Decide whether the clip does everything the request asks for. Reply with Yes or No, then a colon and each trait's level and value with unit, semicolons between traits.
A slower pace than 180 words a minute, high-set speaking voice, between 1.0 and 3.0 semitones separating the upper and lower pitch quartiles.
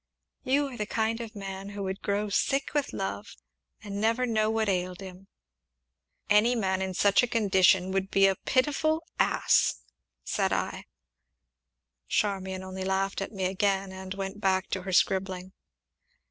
Yes: average, 160 wpm; high, 195 Hz; narrow, 2.5 semitones